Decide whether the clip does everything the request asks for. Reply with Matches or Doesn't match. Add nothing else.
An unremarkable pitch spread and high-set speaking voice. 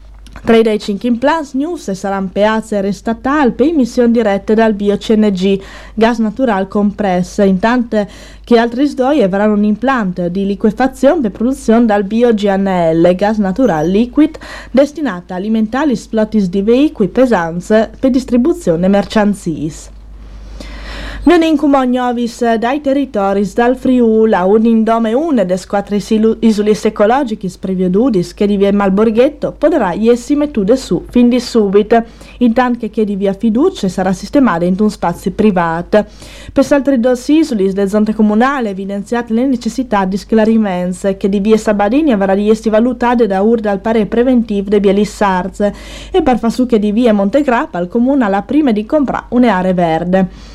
Matches